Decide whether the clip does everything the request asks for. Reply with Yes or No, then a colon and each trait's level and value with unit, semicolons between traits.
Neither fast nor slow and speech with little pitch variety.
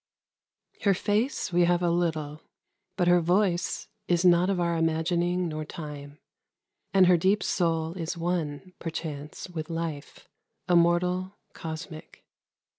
No: slow, 125 wpm; narrow, 2.0 semitones